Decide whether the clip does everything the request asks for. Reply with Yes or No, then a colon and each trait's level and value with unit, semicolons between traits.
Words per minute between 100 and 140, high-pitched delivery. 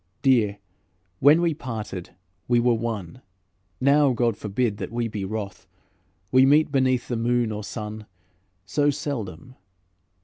No: slow, 135 wpm; low, 120 Hz